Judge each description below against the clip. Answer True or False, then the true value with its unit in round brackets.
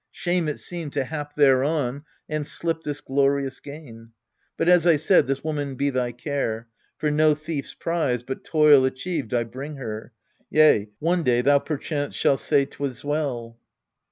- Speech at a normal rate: True (165 wpm)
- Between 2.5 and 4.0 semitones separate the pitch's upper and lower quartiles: True (3.0 semitones)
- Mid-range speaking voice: True (145 Hz)